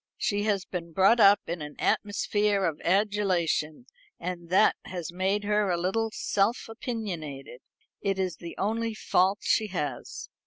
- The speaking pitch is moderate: No, high, 195 Hz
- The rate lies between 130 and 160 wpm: Yes, average, 150 wpm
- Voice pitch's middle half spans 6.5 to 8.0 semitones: No, average, 3.4 semitones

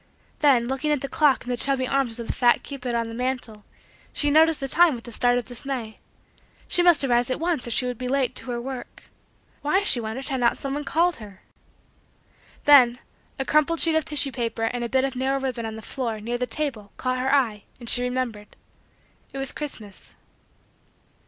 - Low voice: No, very high, 255 Hz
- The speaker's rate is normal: No, fast, 210 wpm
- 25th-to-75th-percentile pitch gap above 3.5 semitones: No, average, 2.8 semitones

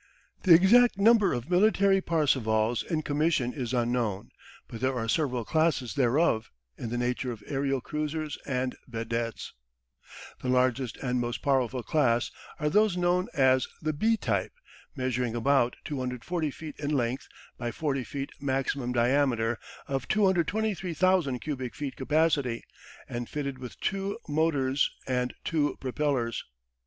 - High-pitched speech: No, low, 135 Hz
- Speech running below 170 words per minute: Yes, slow, 135 wpm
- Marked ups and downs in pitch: No, average, 4.4 semitones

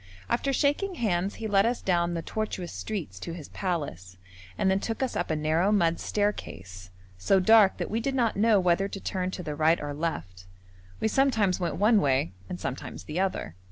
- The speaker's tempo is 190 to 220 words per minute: Yes, average, 200 wpm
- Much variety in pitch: Yes, wide, 5.8 semitones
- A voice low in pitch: No, medium, 185 Hz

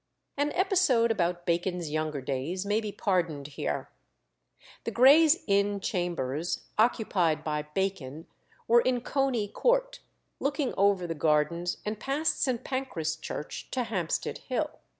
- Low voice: No, high, 195 Hz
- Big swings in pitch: Yes, wide, 7.6 semitones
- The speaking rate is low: Yes, slow, 130 wpm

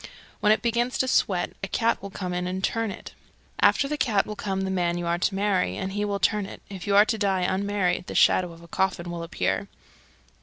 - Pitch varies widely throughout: No, narrow, 2.6 semitones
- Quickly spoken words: Yes, fast, 240 wpm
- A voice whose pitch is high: Yes, high, 195 Hz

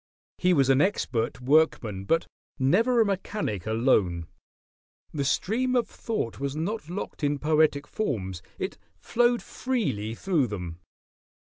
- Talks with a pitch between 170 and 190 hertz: No, medium, 145 Hz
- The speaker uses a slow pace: Yes, slow, 130 wpm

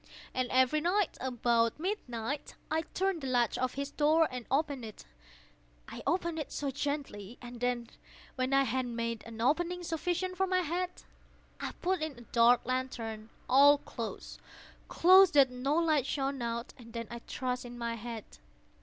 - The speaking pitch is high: Yes, very high, 260 Hz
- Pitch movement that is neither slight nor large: Yes, average, 4.9 semitones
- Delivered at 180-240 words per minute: No, average, 160 wpm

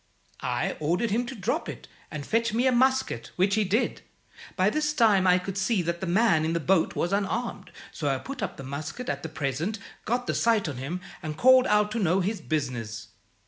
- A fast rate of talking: Yes, fast, 220 wpm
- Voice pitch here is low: No, high, 195 Hz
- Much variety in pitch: Yes, wide, 6.5 semitones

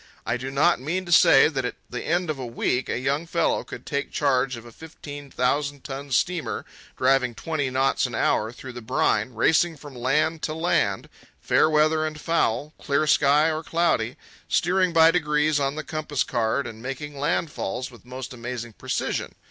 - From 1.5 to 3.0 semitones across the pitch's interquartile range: No, average, 3.8 semitones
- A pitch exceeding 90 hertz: Yes, medium, 140 Hz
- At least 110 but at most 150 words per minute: No, average, 185 wpm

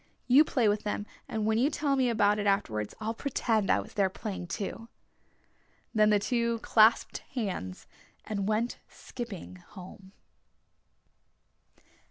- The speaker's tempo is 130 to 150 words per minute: Yes, average, 140 wpm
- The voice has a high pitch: Yes, high, 215 Hz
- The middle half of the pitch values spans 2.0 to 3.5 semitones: Yes, average, 2.9 semitones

